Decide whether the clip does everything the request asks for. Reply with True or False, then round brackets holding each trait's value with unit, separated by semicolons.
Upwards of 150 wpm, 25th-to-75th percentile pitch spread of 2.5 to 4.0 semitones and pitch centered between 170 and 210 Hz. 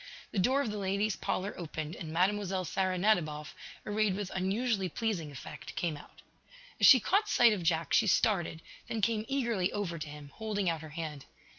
False (185 wpm; 4.6 semitones; 190 Hz)